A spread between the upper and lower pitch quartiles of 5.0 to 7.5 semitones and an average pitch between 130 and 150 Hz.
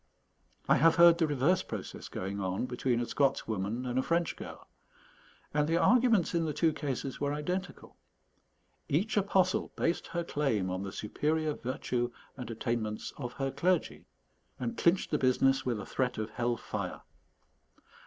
Yes: wide, 5.6 semitones; medium, 140 Hz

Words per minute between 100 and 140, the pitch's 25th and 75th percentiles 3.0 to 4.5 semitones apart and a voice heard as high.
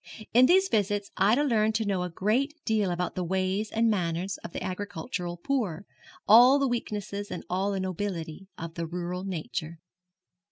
No: average, 170 wpm; average, 3.6 semitones; high, 195 Hz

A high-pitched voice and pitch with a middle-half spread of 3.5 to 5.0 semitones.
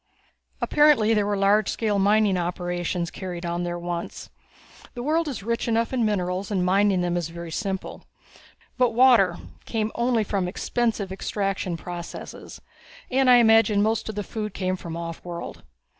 Yes: high, 200 Hz; average, 4.1 semitones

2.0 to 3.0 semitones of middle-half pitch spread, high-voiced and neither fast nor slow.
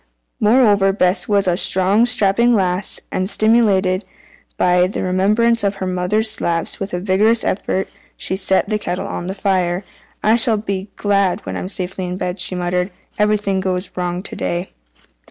Yes: narrow, 2.5 semitones; high, 195 Hz; average, 170 wpm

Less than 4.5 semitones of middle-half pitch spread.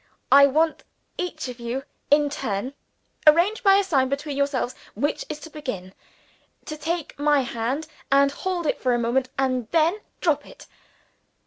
Yes: average, 3.6 semitones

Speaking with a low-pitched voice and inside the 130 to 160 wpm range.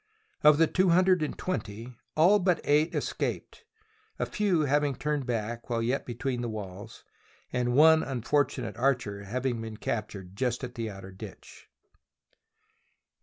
Yes: low, 125 Hz; average, 150 wpm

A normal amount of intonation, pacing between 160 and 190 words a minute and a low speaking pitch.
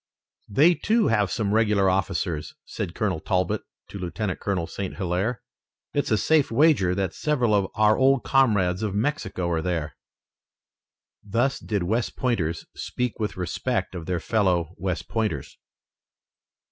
No: average, 4.6 semitones; average, 145 wpm; low, 100 Hz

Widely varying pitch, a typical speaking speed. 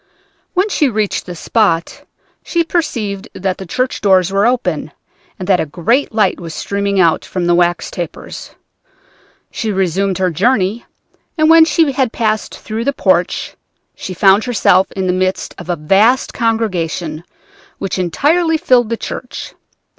No: average, 5.0 semitones; average, 155 wpm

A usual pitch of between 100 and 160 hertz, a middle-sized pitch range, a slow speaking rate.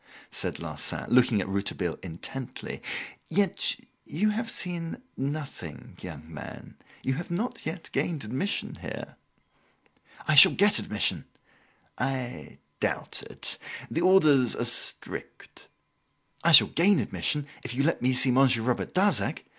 No: low, 135 Hz; wide, 6.2 semitones; slow, 130 wpm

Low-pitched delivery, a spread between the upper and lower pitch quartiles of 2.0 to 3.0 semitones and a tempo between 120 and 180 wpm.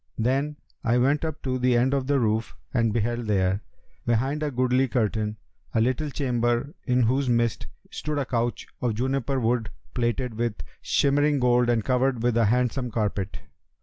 Yes: low, 125 Hz; narrow, 2.5 semitones; average, 170 wpm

